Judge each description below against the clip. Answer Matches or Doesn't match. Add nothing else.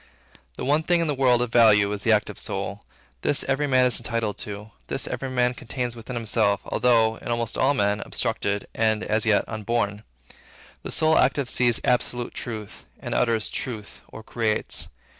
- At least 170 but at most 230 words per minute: Matches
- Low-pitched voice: Matches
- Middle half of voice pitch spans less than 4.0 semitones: Matches